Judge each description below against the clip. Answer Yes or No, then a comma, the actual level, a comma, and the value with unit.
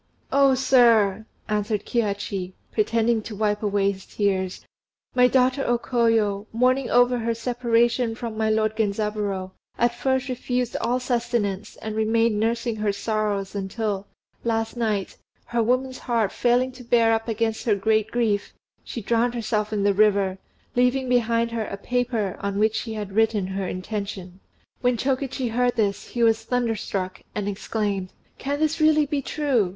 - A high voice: Yes, high, 225 Hz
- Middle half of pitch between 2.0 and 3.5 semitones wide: Yes, average, 3.0 semitones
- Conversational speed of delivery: Yes, average, 155 wpm